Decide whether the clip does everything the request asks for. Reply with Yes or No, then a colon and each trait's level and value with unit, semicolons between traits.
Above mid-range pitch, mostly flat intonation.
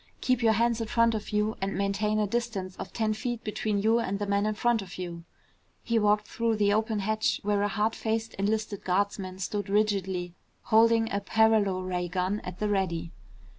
Yes: high, 210 Hz; narrow, 2.2 semitones